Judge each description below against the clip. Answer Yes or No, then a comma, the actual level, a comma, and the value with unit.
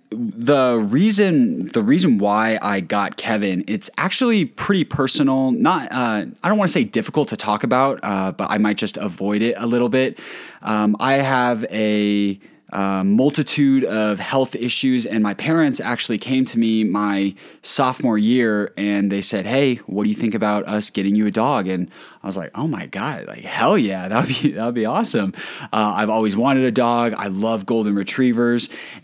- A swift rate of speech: No, average, 190 wpm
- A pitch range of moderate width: Yes, average, 4.0 semitones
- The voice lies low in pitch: Yes, low, 110 Hz